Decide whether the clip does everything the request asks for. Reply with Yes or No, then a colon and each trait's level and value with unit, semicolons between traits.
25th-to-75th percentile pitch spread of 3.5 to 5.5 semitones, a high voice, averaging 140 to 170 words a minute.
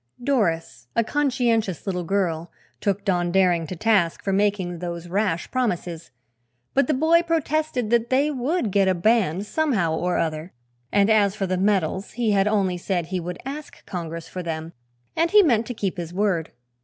No: average, 5.2 semitones; high, 195 Hz; average, 180 wpm